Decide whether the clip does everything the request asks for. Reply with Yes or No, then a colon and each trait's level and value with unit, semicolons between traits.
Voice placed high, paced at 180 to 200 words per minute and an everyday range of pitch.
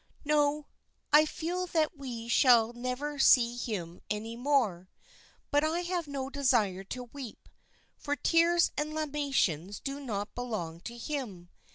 No: very high, 260 Hz; average, 140 wpm; average, 4.9 semitones